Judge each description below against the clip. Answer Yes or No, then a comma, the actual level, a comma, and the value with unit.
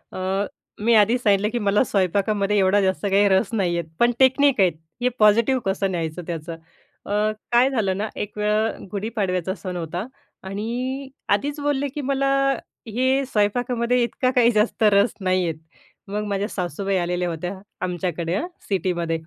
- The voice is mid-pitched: No, high, 205 Hz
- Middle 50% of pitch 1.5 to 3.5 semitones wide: No, average, 4.2 semitones